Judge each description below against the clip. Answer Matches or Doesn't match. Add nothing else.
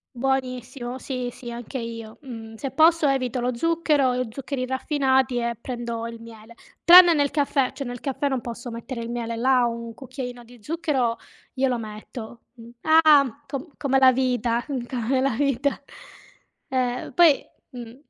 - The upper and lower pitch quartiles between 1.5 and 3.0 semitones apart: Matches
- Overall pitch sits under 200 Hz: Doesn't match